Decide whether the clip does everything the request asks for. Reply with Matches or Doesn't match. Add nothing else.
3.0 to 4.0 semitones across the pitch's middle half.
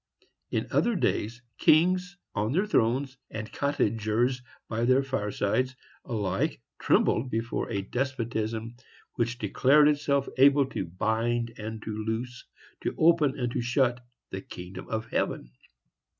Matches